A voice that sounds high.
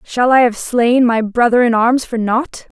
Yes: high, 240 Hz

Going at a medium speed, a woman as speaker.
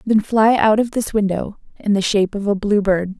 No: fast, 245 wpm; female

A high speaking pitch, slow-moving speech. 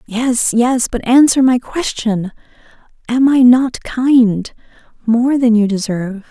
Yes: high, 240 Hz; slow, 125 wpm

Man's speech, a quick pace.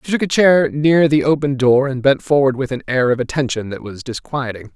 Yes: male; fast, 240 wpm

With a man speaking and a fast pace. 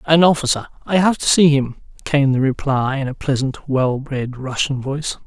No: male; average, 195 wpm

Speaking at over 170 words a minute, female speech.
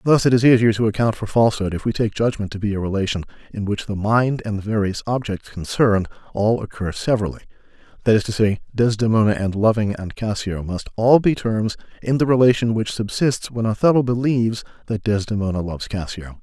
No: average, 195 wpm; male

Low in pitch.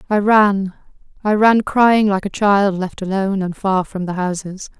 No: high, 200 Hz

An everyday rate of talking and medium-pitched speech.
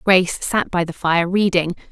Yes: average, 190 wpm; medium, 180 Hz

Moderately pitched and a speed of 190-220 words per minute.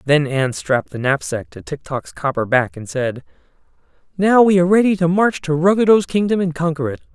Yes: medium, 155 Hz; average, 200 wpm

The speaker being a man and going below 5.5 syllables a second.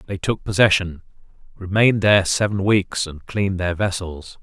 Yes: male; 5.1 syllables/s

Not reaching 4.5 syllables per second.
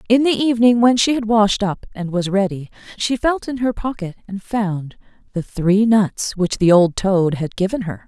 No: 4.7 syllables/s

